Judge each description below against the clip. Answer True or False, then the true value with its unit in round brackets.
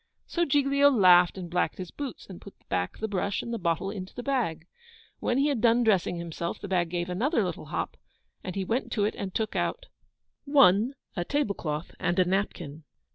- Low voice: False (195 Hz)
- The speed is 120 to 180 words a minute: False (200 wpm)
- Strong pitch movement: True (5.8 semitones)